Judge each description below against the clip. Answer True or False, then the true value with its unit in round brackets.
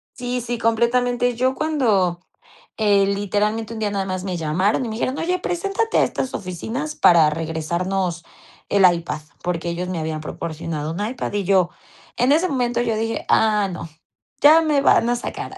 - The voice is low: False (210 Hz)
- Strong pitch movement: True (5.8 semitones)